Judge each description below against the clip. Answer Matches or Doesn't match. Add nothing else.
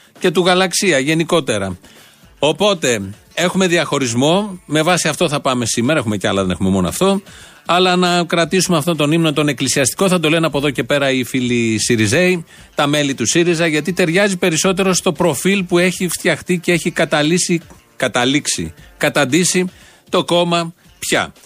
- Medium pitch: Matches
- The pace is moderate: Matches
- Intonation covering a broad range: Doesn't match